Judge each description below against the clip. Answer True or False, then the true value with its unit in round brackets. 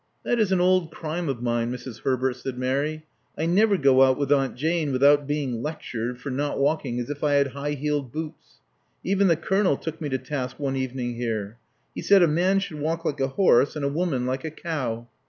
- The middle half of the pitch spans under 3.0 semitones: False (3.8 semitones)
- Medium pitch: True (145 Hz)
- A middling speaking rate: False (225 wpm)